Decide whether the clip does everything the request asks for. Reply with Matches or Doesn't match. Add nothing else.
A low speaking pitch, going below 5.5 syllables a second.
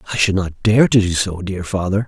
Doesn't match